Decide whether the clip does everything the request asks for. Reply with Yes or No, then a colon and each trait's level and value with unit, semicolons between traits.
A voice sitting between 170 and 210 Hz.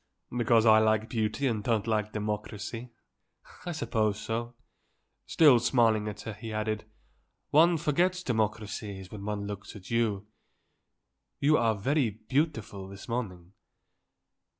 No: low, 110 Hz